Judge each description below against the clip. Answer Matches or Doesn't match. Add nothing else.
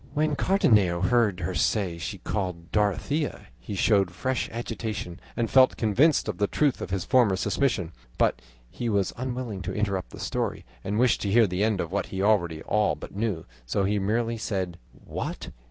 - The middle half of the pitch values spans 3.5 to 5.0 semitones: Matches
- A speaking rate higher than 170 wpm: Matches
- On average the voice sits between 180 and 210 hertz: Doesn't match